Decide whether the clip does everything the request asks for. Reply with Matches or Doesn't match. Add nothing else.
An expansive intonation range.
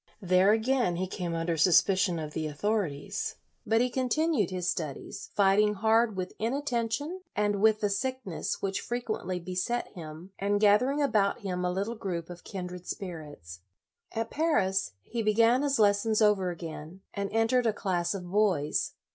Doesn't match